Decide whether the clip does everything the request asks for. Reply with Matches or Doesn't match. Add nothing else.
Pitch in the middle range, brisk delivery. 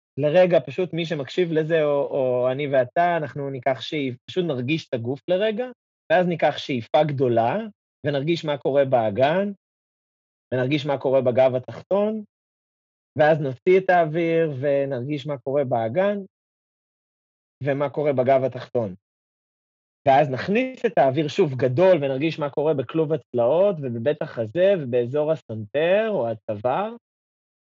Doesn't match